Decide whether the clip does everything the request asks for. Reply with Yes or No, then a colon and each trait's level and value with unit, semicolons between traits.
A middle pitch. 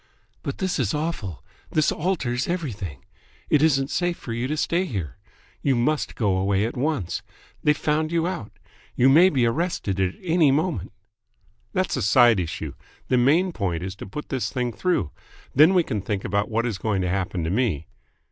No: low, 125 Hz